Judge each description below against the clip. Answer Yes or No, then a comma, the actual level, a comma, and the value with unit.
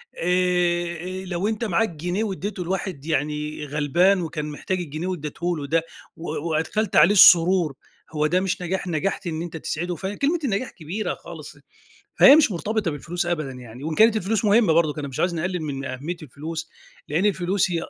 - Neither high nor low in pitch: Yes, medium, 175 Hz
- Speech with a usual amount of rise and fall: Yes, average, 3.6 semitones